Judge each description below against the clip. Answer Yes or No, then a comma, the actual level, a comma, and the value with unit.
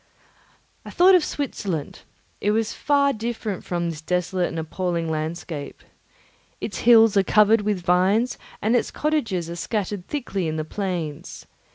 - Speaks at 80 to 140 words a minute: No, average, 150 wpm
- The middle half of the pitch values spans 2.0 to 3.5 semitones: No, average, 4.8 semitones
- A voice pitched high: Yes, high, 195 Hz